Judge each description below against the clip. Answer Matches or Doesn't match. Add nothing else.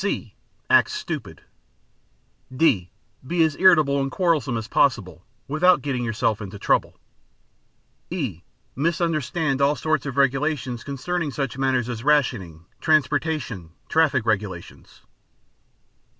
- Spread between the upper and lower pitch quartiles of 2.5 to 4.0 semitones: Doesn't match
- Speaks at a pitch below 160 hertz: Matches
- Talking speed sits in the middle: Doesn't match